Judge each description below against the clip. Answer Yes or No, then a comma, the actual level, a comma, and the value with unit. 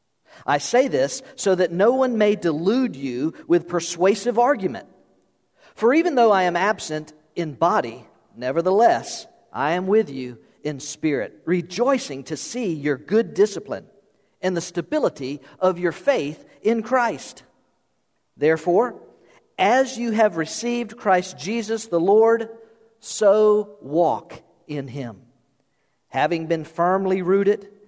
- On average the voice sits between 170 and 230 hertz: Yes, medium, 185 Hz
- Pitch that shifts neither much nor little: No, wide, 5.9 semitones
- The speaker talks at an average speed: No, slow, 125 wpm